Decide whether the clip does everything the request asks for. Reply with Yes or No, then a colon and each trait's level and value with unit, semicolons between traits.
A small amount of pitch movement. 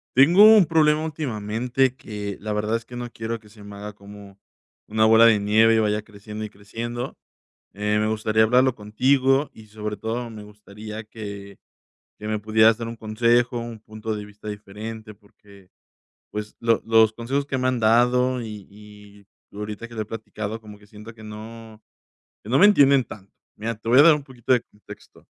Yes: narrow, 2.3 semitones